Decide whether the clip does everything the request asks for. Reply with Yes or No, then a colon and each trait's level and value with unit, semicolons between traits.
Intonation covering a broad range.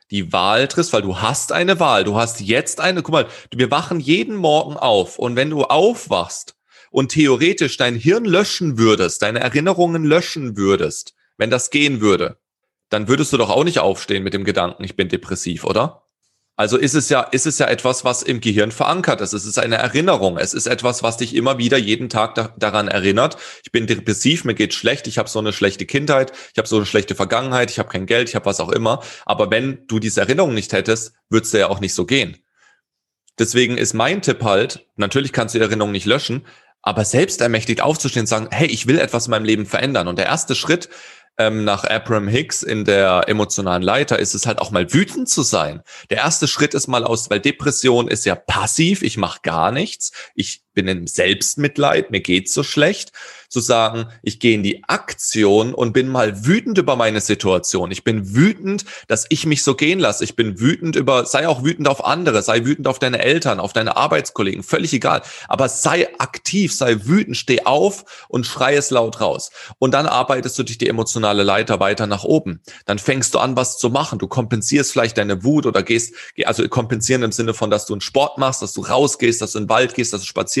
No: average, 4.4 semitones